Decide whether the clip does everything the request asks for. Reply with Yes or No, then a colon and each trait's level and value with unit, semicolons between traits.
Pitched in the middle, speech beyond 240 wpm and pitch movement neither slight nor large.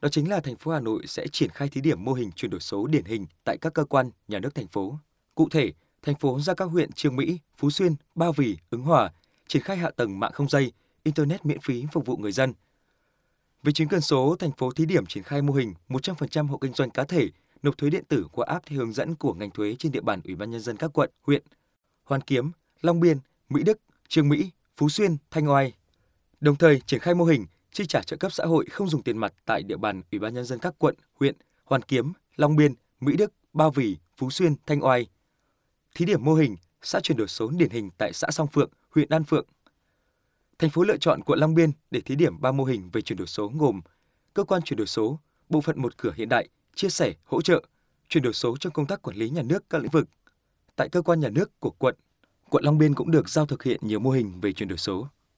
Yes: medium, 145 Hz; fast, 250 wpm; average, 4.0 semitones